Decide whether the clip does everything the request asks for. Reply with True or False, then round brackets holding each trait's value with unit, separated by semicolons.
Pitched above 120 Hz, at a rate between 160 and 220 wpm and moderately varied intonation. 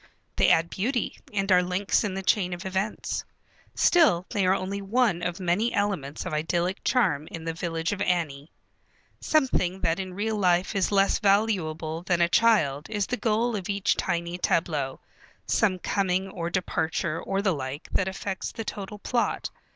True (185 Hz; 175 wpm; 3.2 semitones)